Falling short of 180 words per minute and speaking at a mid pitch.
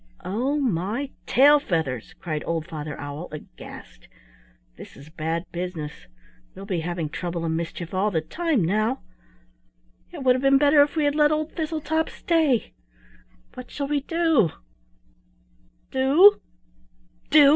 No: average, 140 wpm; high, 220 Hz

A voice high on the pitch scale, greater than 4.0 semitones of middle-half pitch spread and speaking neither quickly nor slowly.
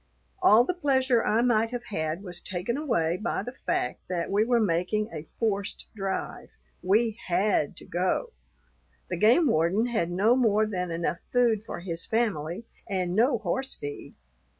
Yes: high, 210 Hz; average, 5.1 semitones; average, 165 wpm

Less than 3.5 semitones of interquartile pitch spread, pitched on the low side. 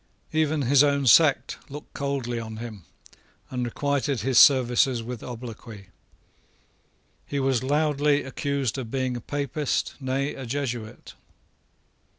Yes: average, 2.9 semitones; low, 130 Hz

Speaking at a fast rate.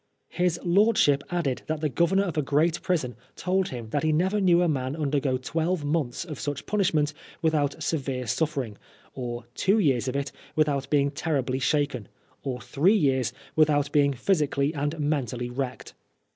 No: average, 165 wpm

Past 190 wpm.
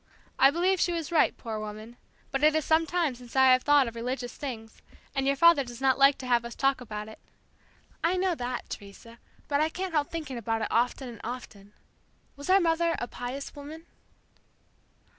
Yes: average, 200 wpm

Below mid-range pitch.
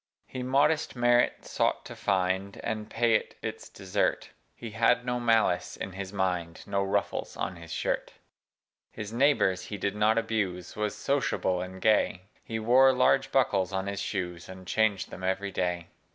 Yes: low, 100 Hz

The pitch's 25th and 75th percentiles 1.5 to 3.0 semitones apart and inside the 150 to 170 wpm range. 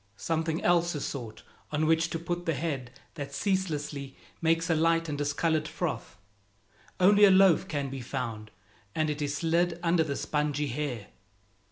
Yes: average, 2.7 semitones; average, 165 wpm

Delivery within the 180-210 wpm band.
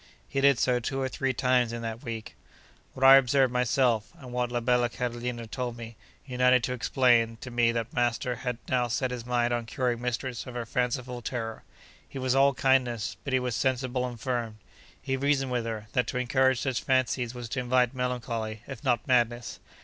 Yes: average, 200 wpm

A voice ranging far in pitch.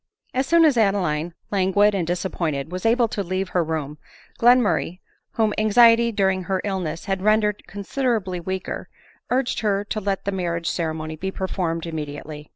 No: average, 4.1 semitones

